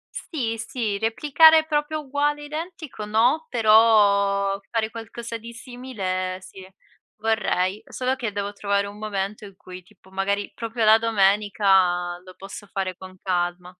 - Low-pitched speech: No, high, 210 Hz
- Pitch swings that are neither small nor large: Yes, average, 3.5 semitones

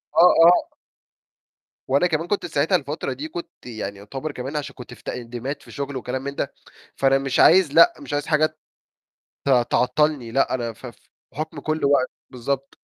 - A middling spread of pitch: Yes, average, 3.4 semitones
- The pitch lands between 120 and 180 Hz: Yes, medium, 140 Hz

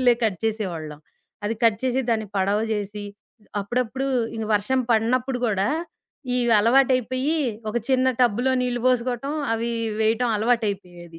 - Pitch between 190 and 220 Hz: No, high, 230 Hz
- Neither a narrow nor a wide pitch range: Yes, average, 3.5 semitones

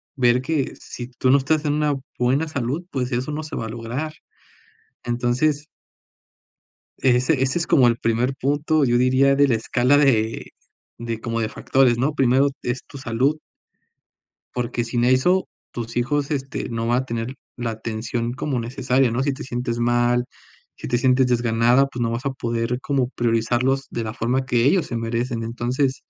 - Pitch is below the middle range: Yes, low, 125 Hz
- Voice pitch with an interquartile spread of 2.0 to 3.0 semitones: Yes, narrow, 2.5 semitones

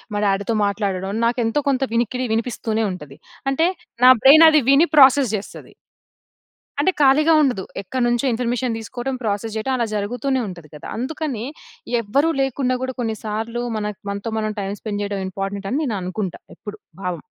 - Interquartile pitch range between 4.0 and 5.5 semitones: Yes, average, 4.4 semitones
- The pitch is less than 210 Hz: No, high, 230 Hz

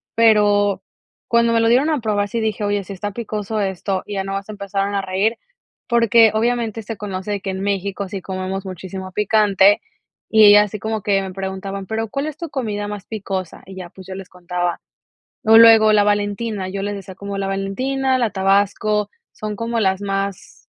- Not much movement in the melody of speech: Yes, narrow, 2.2 semitones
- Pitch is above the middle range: Yes, high, 205 Hz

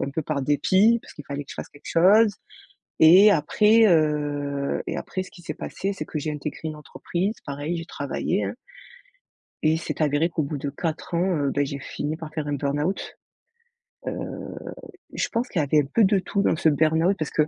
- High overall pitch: No, medium, 155 Hz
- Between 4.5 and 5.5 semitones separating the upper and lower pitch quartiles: No, average, 4.0 semitones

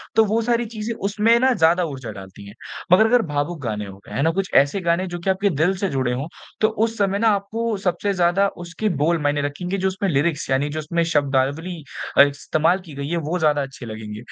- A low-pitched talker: No, medium, 170 Hz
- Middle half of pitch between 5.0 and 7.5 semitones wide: Yes, wide, 5.6 semitones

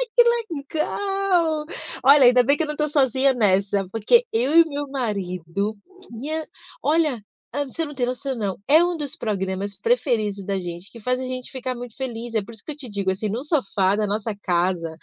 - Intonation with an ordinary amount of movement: No, wide, 6.6 semitones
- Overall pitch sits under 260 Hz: Yes, high, 245 Hz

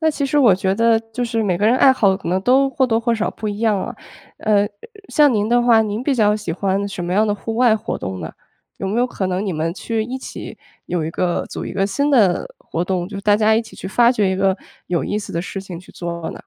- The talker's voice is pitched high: Yes, high, 210 Hz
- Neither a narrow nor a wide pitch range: Yes, average, 3.6 semitones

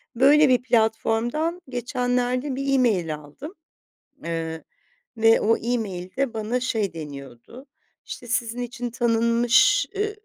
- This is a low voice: No, high, 235 Hz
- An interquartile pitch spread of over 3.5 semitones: No, average, 3.1 semitones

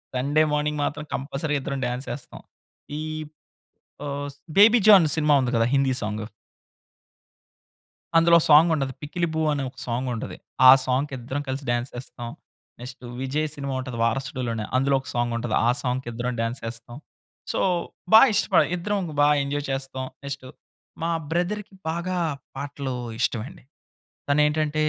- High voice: No, medium, 140 Hz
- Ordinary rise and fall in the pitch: Yes, average, 3.5 semitones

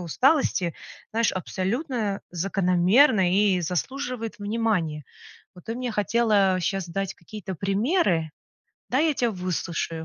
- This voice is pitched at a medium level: No, high, 195 Hz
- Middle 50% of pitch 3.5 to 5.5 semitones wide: Yes, average, 4.4 semitones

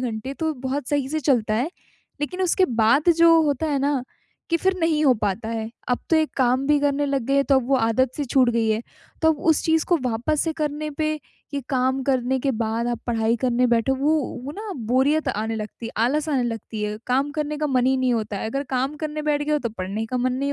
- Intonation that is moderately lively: Yes, average, 4.0 semitones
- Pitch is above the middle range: Yes, very high, 265 Hz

